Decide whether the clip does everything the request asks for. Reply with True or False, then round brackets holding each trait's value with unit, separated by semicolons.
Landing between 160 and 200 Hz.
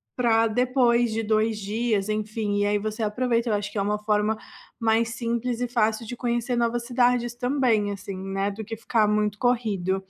False (225 Hz)